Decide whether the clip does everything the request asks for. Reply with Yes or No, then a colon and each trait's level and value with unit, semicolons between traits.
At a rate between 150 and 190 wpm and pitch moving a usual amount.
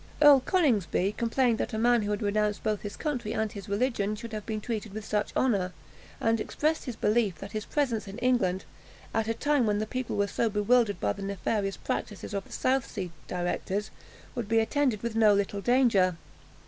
No: average, 200 wpm; average, 3.0 semitones